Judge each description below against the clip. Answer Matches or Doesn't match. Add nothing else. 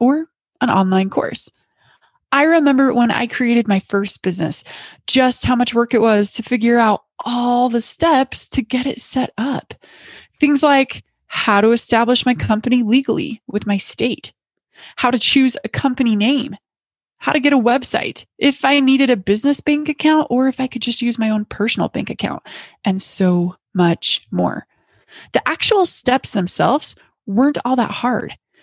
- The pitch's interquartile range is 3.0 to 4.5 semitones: Matches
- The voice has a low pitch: Doesn't match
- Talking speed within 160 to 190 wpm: Matches